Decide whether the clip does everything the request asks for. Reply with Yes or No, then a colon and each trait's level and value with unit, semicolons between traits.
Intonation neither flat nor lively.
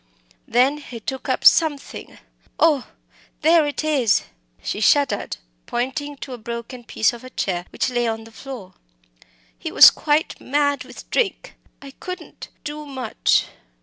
Yes: average, 3.9 semitones